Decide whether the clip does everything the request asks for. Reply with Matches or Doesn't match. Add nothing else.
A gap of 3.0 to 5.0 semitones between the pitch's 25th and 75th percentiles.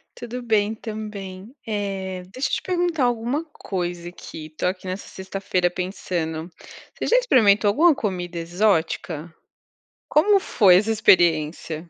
Matches